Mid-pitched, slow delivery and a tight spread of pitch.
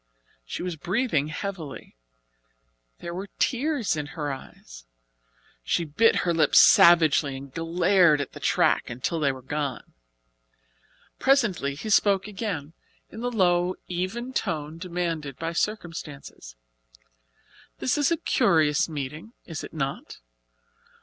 No: medium, 165 Hz; slow, 125 wpm; average, 5.3 semitones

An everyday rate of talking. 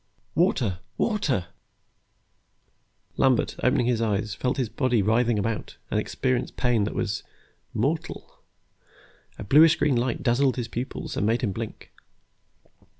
No: slow, 130 wpm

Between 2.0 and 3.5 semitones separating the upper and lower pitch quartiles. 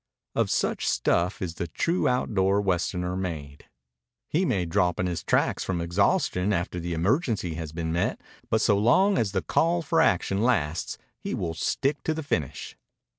No: average, 5.0 semitones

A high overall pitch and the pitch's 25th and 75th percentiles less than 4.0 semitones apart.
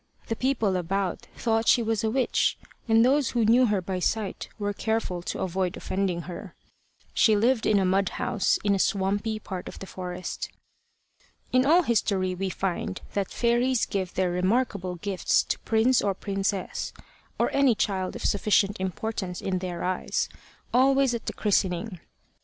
Yes: high, 200 Hz; average, 3.4 semitones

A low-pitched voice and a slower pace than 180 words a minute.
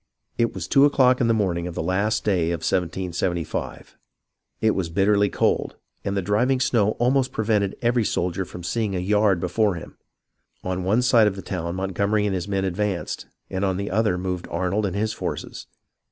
No: low, 100 Hz; average, 190 wpm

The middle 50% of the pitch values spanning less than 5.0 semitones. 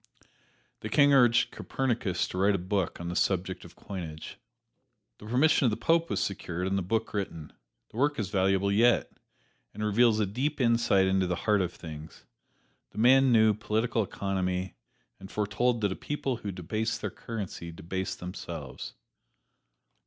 Yes: average, 3.9 semitones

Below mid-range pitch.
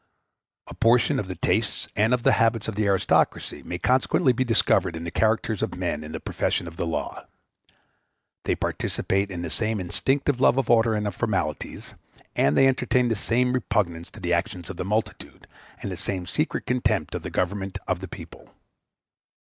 Yes: low, 105 Hz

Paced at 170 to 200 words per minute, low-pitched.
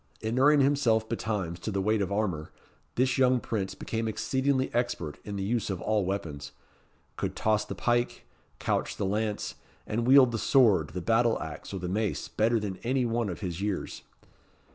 Yes: average, 180 wpm; low, 110 Hz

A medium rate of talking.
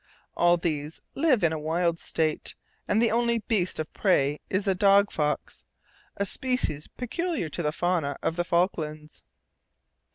Yes: average, 155 wpm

